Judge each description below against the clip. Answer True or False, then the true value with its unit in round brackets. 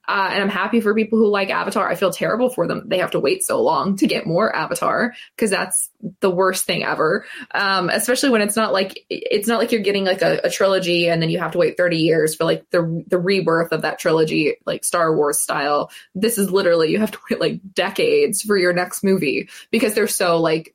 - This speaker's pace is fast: True (235 wpm)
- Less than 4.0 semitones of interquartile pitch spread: False (4.4 semitones)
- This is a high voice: True (195 Hz)